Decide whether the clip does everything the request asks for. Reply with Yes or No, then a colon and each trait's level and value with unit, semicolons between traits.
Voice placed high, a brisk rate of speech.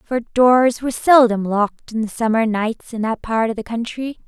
Yes: high, 230 Hz; fast, 210 wpm